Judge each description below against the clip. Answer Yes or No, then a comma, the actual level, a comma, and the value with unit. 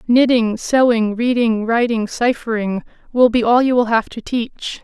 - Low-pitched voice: No, high, 235 Hz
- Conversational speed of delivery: Yes, average, 160 wpm